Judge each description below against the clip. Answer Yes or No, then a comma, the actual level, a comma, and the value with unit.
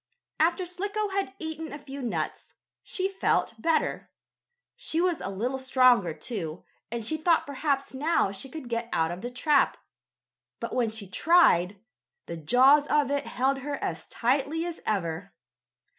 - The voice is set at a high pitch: Yes, very high, 270 Hz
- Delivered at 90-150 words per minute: No, average, 160 wpm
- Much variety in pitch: Yes, wide, 6.2 semitones